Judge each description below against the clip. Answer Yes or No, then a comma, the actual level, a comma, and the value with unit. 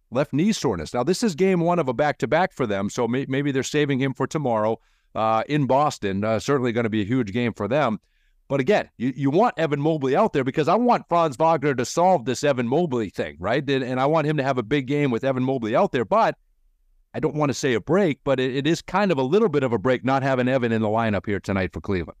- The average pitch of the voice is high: No, low, 135 Hz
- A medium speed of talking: No, fast, 275 wpm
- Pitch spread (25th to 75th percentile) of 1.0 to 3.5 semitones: No, average, 4.3 semitones